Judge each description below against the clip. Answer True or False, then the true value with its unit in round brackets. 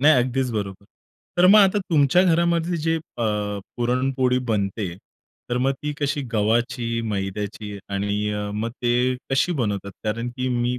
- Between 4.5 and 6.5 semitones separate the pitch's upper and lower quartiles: True (5.3 semitones)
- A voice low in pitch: True (120 Hz)